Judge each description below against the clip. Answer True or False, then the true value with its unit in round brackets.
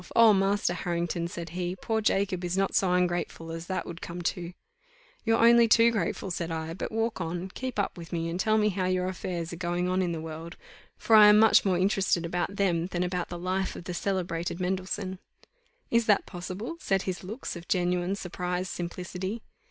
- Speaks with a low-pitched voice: False (180 Hz)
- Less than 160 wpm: False (205 wpm)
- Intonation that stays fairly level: True (2.3 semitones)